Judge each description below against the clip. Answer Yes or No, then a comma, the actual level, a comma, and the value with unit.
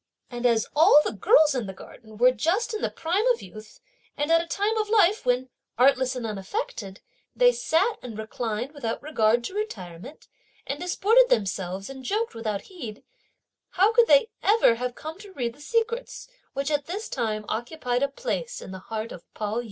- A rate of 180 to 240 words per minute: Yes, average, 190 wpm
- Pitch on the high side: Yes, very high, 270 Hz